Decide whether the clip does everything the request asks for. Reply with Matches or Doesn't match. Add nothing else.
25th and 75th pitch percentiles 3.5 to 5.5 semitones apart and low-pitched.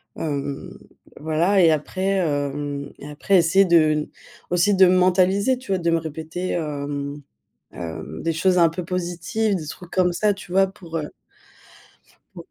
Doesn't match